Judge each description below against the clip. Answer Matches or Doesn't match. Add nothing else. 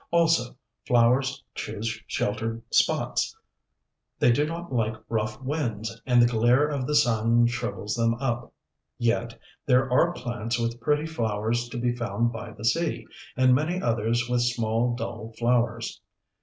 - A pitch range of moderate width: Doesn't match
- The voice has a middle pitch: Doesn't match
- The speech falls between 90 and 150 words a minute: Matches